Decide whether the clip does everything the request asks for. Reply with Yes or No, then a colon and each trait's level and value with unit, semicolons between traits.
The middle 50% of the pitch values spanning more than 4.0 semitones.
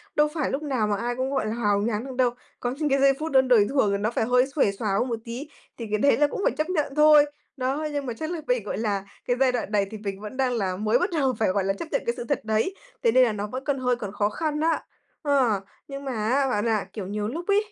Yes: average, 4.6 semitones